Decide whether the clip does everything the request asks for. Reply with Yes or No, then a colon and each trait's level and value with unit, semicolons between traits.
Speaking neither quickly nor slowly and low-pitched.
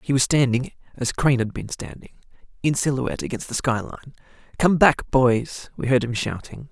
Yes: average, 190 wpm; low, 130 Hz